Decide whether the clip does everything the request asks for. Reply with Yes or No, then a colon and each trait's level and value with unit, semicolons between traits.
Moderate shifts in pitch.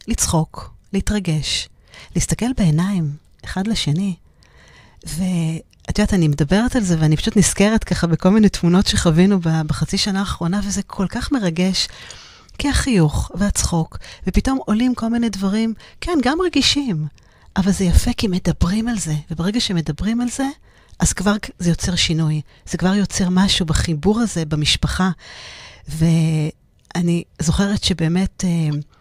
Yes: average, 4.2 semitones